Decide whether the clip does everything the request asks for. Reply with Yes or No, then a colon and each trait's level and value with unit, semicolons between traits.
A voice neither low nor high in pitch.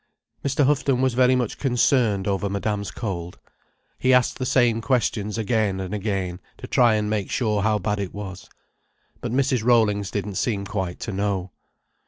No: low, 105 Hz